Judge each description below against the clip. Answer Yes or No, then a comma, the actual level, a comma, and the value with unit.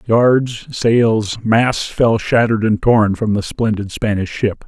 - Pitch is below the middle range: Yes, low, 110 Hz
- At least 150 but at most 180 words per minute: Yes, average, 155 wpm